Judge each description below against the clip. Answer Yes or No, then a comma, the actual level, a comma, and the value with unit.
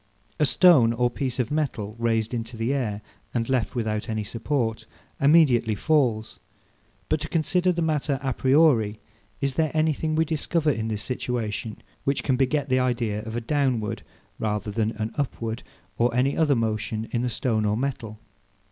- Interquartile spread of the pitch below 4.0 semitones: No, average, 4.3 semitones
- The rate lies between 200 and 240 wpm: No, average, 170 wpm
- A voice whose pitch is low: Yes, low, 125 Hz